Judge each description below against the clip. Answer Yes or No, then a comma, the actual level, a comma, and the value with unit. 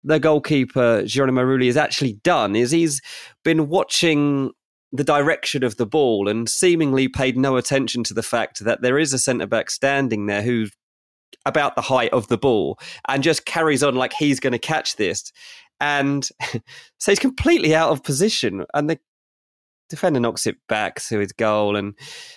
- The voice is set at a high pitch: No, low, 135 Hz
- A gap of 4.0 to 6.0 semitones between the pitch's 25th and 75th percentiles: Yes, average, 4.6 semitones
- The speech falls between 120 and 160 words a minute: No, average, 175 wpm